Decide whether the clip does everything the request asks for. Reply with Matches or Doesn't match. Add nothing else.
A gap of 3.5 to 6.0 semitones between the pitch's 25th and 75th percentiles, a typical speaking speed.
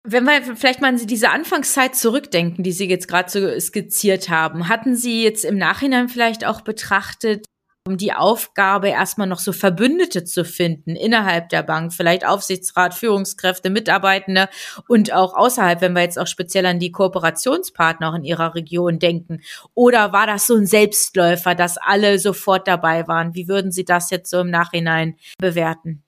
Matches